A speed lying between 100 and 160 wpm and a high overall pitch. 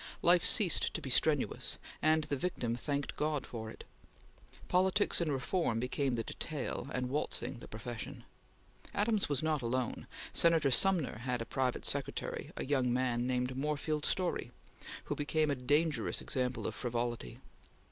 No: average, 150 wpm; low, 135 Hz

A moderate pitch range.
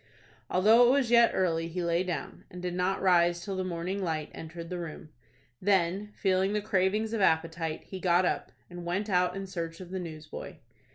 No: narrow, 2.3 semitones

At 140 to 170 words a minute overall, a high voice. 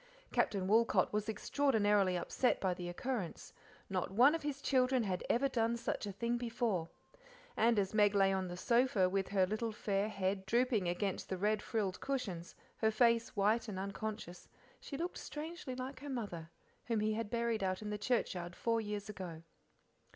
No: average, 180 wpm; high, 215 Hz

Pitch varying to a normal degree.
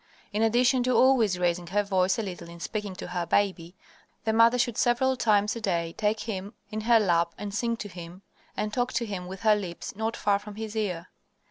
Yes: average, 3.7 semitones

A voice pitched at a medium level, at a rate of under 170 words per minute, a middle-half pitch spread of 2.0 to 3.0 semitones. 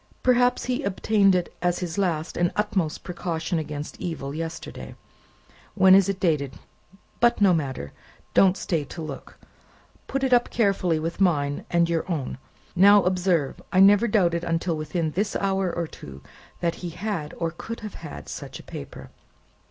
No: medium, 175 Hz; average, 160 wpm; average, 3.6 semitones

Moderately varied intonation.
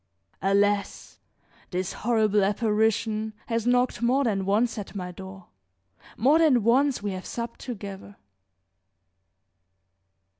Yes: average, 3.2 semitones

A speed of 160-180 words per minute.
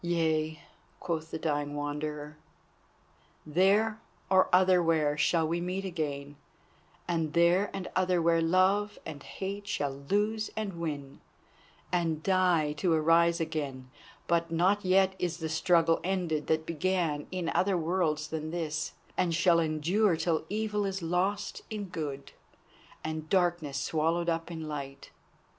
No: slow, 135 wpm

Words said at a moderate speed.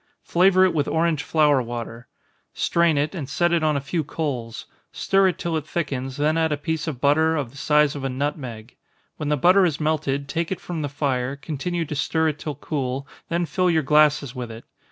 No: fast, 215 wpm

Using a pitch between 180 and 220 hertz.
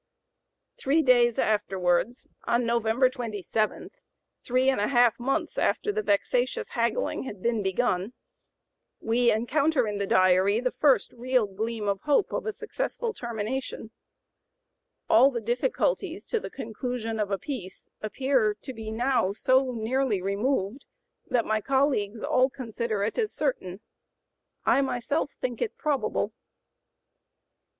No: high, 240 Hz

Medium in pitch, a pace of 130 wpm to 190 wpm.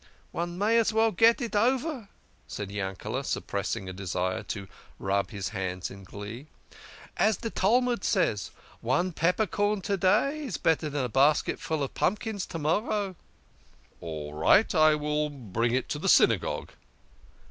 Yes: medium, 155 Hz; average, 170 wpm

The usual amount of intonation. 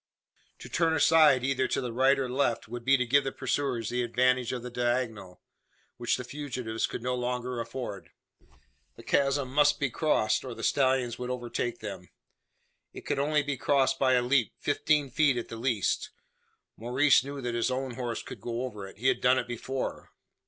No: narrow, 2.2 semitones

